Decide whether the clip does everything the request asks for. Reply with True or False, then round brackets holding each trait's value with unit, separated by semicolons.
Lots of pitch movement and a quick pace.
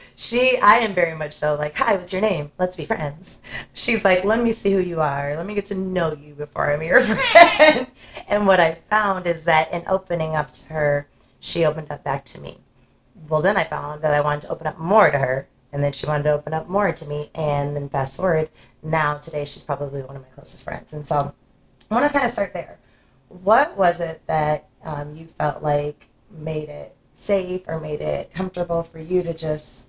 False (3.7 semitones; 225 wpm)